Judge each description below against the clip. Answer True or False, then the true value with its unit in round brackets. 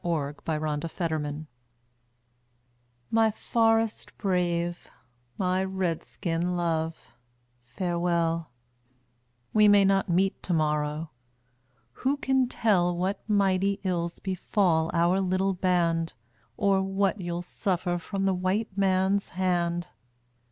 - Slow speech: True (115 wpm)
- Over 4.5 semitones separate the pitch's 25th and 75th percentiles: False (2.6 semitones)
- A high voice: False (180 Hz)